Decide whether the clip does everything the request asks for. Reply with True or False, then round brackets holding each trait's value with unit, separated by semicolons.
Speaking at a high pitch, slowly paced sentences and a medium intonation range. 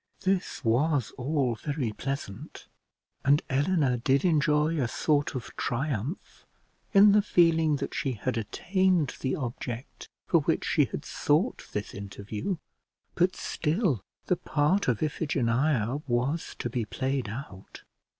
False (140 Hz; 130 wpm; 5.0 semitones)